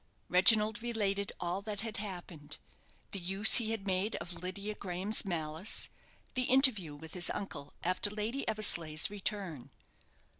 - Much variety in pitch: No, average, 3.6 semitones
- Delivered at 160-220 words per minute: No, average, 140 wpm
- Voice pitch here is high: Yes, high, 195 Hz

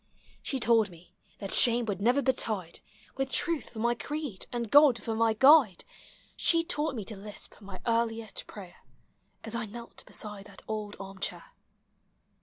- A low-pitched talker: No, high, 225 Hz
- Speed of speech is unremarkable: Yes, average, 165 wpm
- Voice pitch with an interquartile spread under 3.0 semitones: No, average, 3.5 semitones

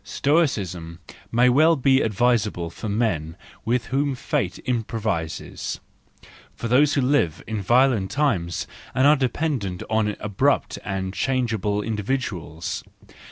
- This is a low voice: Yes, low, 115 Hz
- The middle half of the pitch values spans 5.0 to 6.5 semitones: Yes, wide, 5.6 semitones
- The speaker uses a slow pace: Yes, slow, 120 wpm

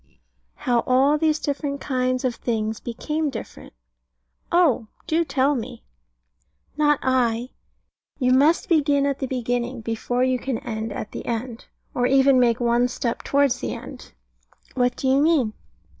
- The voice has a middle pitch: No, very high, 255 Hz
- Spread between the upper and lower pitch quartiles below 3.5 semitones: Yes, average, 2.9 semitones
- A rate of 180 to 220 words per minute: No, average, 150 wpm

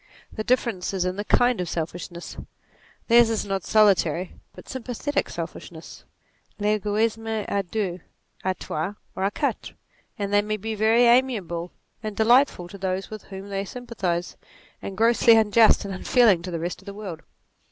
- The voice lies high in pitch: Yes, high, 205 Hz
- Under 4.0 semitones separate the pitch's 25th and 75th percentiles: Yes, average, 3.3 semitones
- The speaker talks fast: No, average, 165 wpm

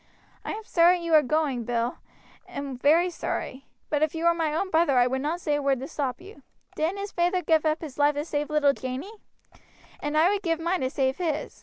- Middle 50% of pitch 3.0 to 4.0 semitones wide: Yes, average, 3.6 semitones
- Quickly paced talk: Yes, fast, 225 wpm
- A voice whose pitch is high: Yes, very high, 310 Hz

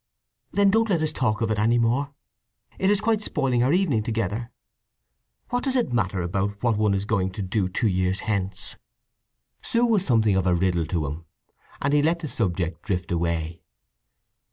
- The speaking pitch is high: No, low, 110 Hz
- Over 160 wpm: Yes, average, 185 wpm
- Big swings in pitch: Yes, wide, 7.6 semitones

